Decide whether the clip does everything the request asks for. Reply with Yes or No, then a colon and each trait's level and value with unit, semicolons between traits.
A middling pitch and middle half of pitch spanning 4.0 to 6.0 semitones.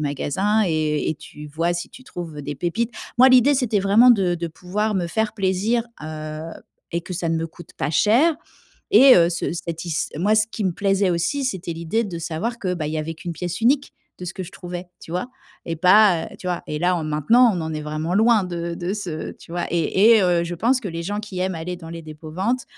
Yes: medium, 180 Hz; average, 4.3 semitones